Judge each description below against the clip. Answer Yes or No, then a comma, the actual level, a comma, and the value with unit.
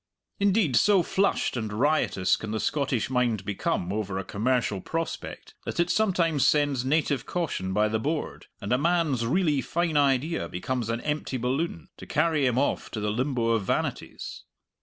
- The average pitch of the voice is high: No, low, 130 Hz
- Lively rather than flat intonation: Yes, wide, 6.3 semitones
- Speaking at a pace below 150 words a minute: No, average, 170 wpm